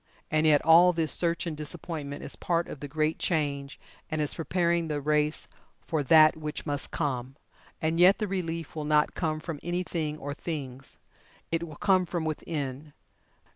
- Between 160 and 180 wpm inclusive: Yes, average, 175 wpm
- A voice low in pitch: No, medium, 155 Hz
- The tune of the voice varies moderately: No, narrow, 2.2 semitones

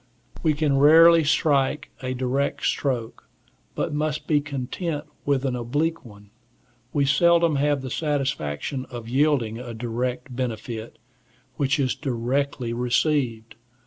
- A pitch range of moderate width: Yes, average, 3.4 semitones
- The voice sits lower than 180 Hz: Yes, low, 135 Hz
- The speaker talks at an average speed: No, slow, 125 wpm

